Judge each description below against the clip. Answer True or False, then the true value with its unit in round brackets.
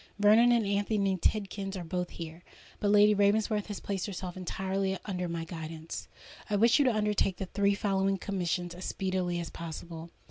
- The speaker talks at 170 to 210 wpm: True (175 wpm)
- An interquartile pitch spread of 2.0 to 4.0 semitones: True (2.6 semitones)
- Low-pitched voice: False (195 Hz)